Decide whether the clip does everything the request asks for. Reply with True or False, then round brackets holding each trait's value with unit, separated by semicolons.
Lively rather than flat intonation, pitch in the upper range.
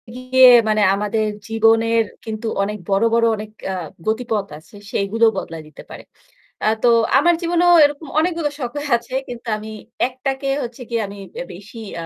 False (3.4 semitones; 230 Hz)